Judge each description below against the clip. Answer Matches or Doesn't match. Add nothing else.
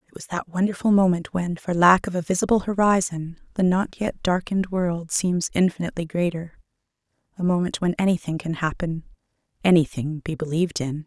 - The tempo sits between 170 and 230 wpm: Doesn't match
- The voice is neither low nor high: Matches